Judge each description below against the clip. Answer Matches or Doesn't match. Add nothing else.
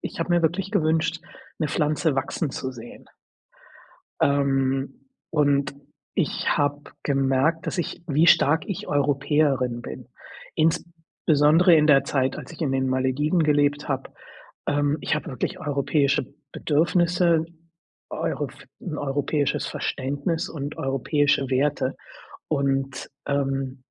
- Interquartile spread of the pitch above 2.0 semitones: Matches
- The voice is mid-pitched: Matches